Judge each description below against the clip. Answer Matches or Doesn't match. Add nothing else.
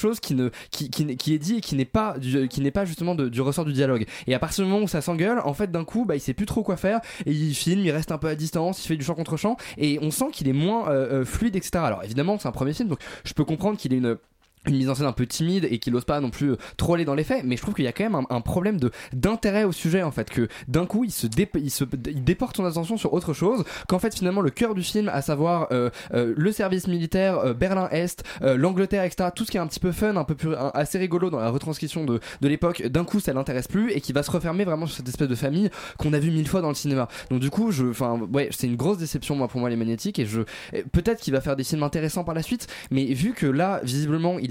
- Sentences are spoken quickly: Matches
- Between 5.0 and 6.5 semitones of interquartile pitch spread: Matches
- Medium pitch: Matches